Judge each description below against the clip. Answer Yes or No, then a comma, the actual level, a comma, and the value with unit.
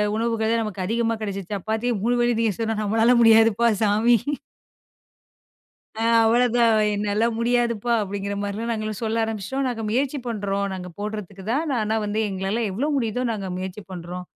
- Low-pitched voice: No, high, 220 Hz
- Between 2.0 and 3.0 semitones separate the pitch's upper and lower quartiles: Yes, narrow, 2.6 semitones